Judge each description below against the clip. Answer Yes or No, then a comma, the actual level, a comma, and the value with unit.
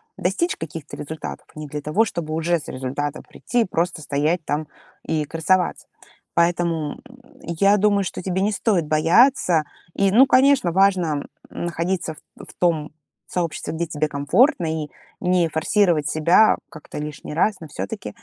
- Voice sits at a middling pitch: Yes, medium, 170 Hz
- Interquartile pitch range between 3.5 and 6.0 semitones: Yes, average, 3.8 semitones